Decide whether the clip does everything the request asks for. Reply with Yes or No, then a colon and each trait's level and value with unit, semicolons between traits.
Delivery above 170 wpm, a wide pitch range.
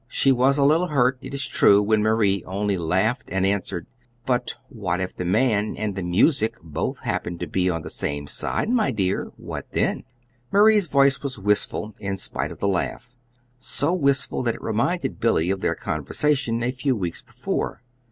Yes: average, 185 wpm; wide, 6.1 semitones